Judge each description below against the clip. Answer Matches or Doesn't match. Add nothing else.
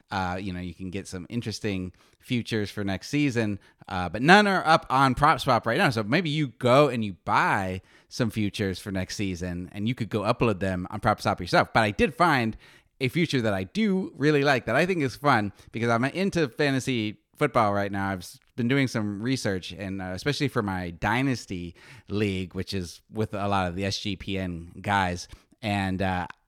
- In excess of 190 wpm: Matches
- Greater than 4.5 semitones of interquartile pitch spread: Matches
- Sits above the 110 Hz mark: Doesn't match